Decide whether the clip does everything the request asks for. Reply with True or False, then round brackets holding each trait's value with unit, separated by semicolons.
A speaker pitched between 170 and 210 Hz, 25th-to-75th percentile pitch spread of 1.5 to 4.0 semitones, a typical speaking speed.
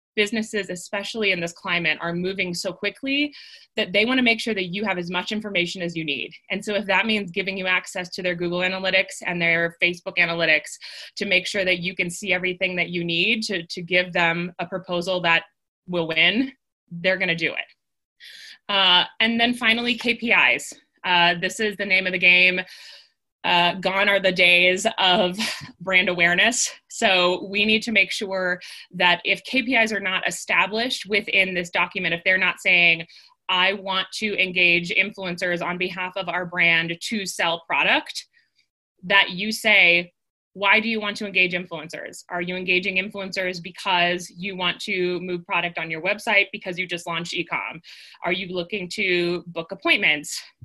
True (185 Hz; 2.4 semitones; 180 wpm)